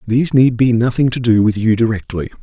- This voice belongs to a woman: No, male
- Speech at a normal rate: No, fast, 225 wpm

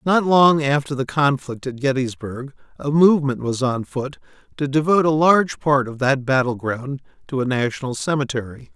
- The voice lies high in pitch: No, medium, 140 Hz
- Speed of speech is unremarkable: Yes, average, 170 wpm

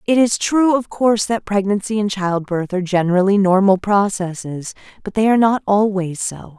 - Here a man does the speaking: No, female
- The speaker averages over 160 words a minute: Yes, average, 175 wpm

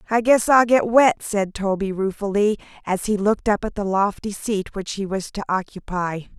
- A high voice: Yes, high, 205 Hz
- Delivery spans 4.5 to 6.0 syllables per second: Yes, 4.9 syllables/s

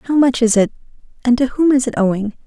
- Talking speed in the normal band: No, fast, 245 wpm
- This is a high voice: Yes, high, 245 Hz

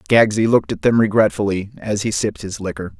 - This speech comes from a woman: No, male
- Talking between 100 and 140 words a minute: No, average, 200 wpm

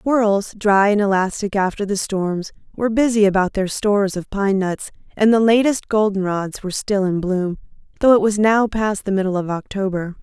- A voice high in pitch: Yes, high, 200 Hz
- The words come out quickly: No, average, 190 wpm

